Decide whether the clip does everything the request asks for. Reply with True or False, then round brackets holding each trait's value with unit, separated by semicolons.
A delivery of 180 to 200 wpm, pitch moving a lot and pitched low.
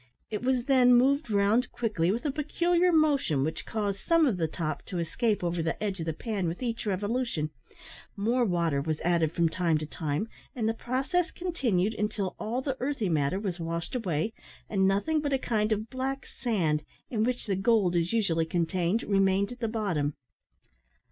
False (190 wpm; 6.4 semitones; 210 Hz)